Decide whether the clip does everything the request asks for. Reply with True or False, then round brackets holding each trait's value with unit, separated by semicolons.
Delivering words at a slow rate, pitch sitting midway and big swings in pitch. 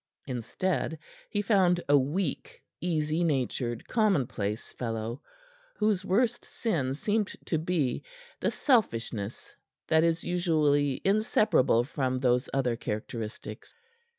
True (105 wpm; 150 Hz; 6.9 semitones)